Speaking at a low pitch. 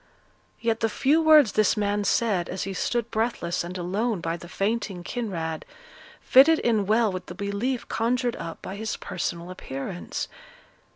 No: high, 210 Hz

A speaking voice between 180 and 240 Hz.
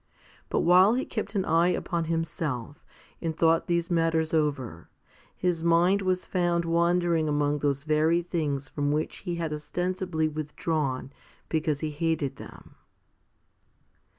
No: medium, 165 Hz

